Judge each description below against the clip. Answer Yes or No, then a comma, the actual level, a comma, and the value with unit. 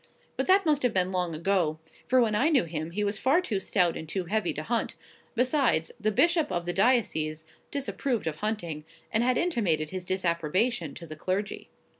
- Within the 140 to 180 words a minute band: No, average, 195 wpm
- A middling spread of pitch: No, wide, 6.6 semitones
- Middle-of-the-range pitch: No, high, 195 Hz